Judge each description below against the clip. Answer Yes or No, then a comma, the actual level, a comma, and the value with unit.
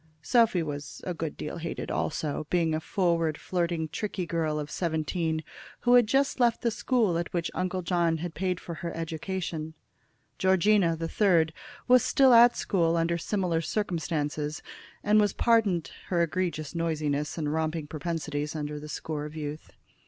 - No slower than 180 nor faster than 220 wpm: No, average, 160 wpm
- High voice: No, medium, 165 Hz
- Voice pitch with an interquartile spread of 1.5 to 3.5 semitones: Yes, average, 3.1 semitones